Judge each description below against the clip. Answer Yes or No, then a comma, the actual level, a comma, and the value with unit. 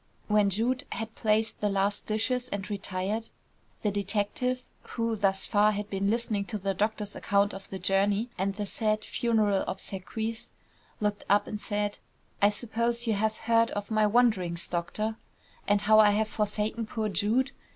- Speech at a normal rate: Yes, average, 165 wpm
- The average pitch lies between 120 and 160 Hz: No, high, 210 Hz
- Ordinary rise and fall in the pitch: No, narrow, 1.8 semitones